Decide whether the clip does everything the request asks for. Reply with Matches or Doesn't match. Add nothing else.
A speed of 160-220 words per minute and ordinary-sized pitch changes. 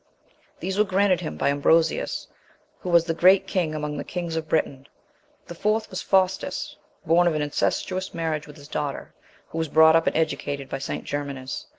Matches